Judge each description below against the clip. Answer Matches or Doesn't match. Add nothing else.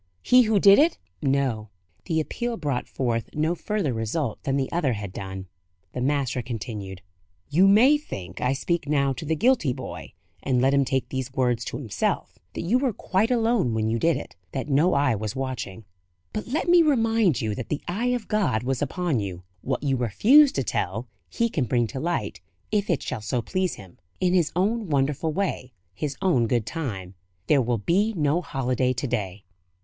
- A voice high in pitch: Doesn't match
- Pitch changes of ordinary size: Doesn't match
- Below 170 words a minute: Doesn't match